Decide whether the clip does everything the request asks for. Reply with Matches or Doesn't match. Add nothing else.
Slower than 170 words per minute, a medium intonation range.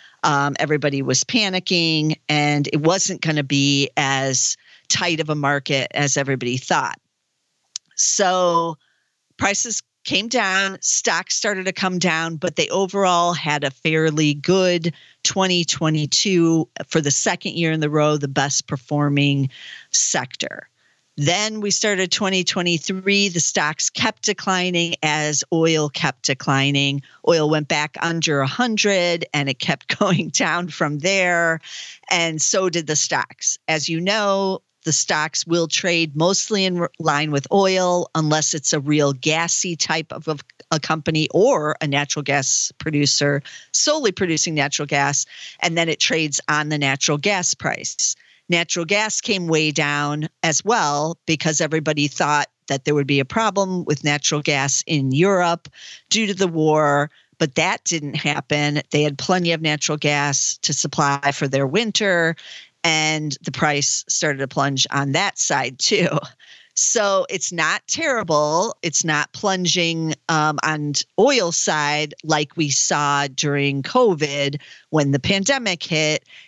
Matches